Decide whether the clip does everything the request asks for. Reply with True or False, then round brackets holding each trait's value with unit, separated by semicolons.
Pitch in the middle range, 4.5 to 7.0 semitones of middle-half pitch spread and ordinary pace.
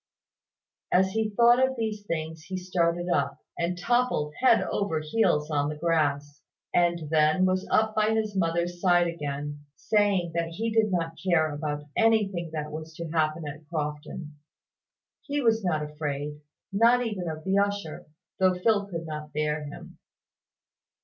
True (170 Hz; 4.8 semitones; 155 wpm)